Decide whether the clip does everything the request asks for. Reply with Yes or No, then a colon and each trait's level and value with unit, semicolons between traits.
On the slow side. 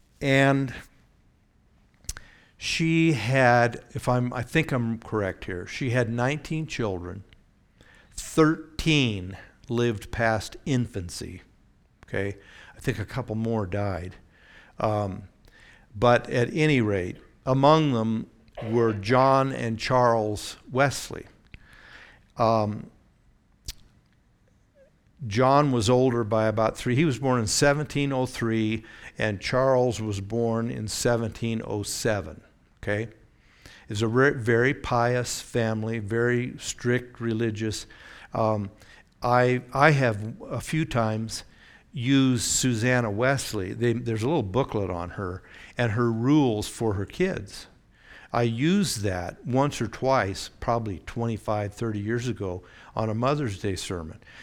Yes: slow, 115 wpm